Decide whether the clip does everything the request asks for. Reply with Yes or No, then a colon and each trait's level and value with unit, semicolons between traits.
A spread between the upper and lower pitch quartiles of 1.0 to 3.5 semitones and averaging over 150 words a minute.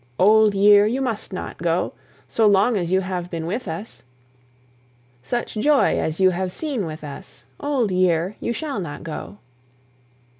No: average, 4.1 semitones; average, 160 wpm